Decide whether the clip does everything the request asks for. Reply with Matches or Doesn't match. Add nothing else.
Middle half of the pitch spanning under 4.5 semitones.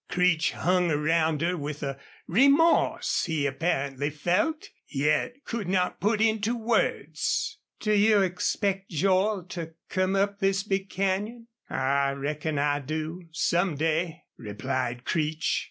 Doesn't match